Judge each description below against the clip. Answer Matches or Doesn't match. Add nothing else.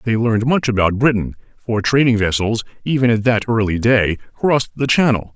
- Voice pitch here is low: Matches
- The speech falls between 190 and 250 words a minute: Doesn't match